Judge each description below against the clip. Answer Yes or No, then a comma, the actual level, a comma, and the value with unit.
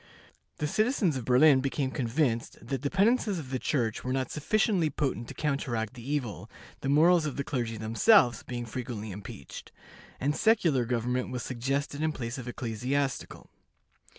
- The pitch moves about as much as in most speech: Yes, average, 4.0 semitones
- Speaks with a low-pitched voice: Yes, low, 130 Hz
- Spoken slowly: No, average, 160 wpm